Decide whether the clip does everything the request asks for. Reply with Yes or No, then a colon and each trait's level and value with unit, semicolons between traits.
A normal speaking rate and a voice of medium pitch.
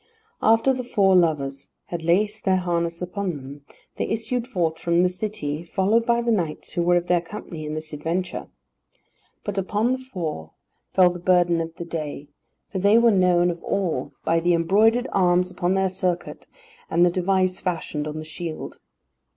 Yes: average, 180 wpm; medium, 180 Hz